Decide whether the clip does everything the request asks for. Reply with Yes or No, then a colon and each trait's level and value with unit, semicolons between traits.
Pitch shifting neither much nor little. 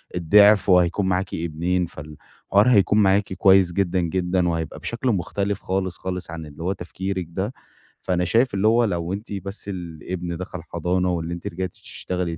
No: narrow, 2.3 semitones